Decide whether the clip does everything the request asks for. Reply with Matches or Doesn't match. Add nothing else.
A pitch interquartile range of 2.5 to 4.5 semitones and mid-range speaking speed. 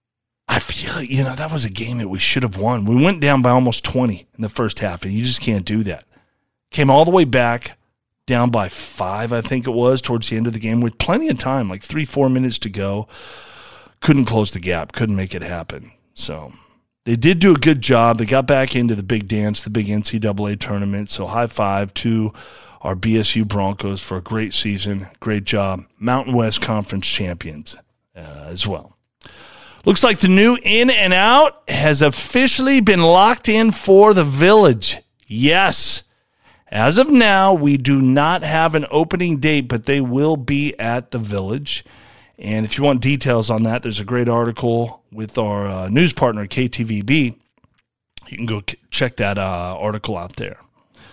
Doesn't match